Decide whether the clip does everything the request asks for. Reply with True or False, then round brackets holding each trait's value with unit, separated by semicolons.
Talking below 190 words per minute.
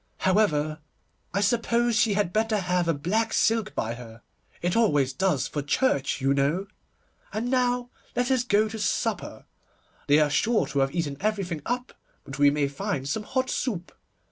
True (170 wpm)